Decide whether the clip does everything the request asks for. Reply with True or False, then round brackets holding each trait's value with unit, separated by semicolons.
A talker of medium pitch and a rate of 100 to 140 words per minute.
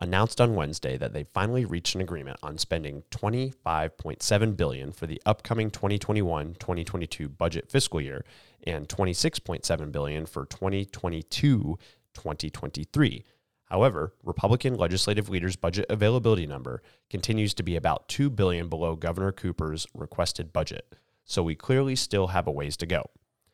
False (90 Hz; 135 wpm)